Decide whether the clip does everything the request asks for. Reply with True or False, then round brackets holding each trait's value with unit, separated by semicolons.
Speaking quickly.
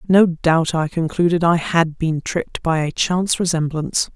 False (175 wpm)